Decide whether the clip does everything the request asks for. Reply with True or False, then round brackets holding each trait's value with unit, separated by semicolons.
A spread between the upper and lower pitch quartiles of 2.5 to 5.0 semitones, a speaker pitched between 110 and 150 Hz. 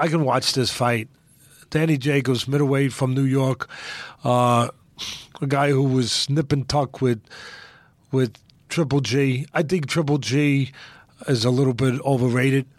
False (2.1 semitones; 135 Hz)